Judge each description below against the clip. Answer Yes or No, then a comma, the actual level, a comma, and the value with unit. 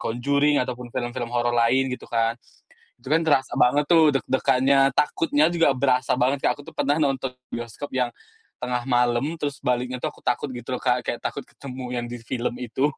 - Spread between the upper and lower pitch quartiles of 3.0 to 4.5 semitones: No, narrow, 2.4 semitones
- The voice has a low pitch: Yes, low, 125 Hz